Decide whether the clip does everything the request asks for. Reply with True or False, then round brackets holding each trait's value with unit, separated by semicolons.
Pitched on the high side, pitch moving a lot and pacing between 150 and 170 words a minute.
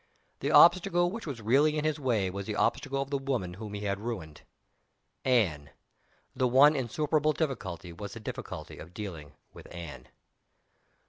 False (115 Hz; 7.3 semitones; 160 wpm)